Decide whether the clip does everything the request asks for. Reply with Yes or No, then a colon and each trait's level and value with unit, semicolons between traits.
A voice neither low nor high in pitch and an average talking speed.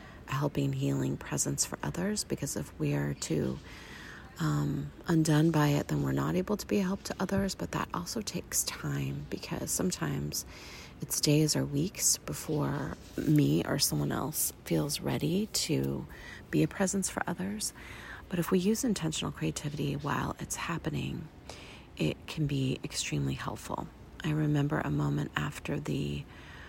Yes: medium, 145 Hz; average, 155 wpm